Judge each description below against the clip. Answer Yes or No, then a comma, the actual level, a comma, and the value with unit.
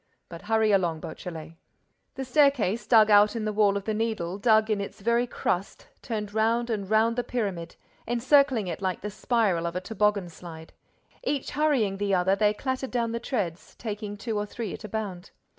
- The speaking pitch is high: Yes, high, 210 Hz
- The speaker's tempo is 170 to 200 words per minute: Yes, average, 190 wpm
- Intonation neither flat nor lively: Yes, average, 3.2 semitones